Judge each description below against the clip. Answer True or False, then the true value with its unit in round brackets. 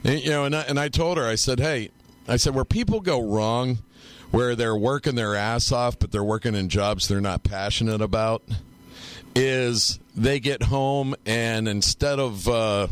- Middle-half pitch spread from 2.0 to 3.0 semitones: False (3.9 semitones)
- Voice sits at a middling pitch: False (115 Hz)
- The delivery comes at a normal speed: True (190 wpm)